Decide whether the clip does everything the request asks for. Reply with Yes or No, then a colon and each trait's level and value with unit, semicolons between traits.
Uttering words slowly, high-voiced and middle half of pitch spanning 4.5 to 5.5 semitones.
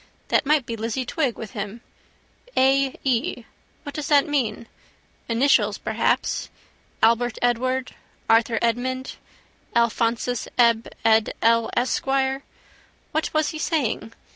No: slow, 115 wpm; high, 245 Hz; average, 2.8 semitones